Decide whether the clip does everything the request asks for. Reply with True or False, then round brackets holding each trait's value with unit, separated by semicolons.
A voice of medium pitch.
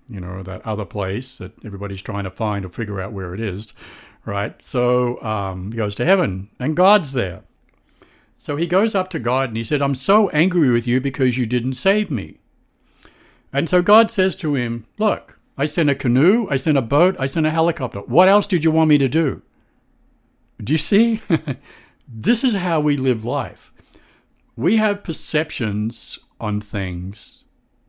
False (130 Hz)